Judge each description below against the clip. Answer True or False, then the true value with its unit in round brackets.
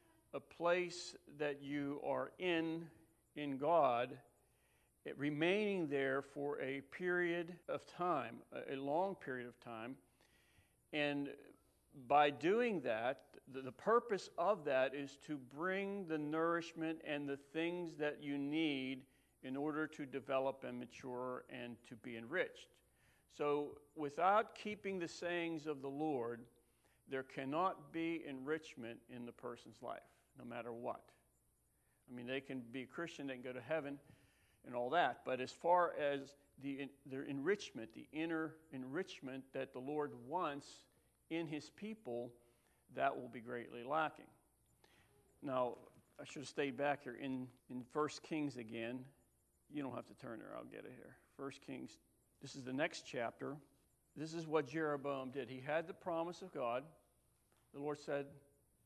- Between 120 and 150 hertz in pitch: True (140 Hz)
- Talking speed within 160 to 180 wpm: False (150 wpm)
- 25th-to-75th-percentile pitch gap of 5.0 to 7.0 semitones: False (3.8 semitones)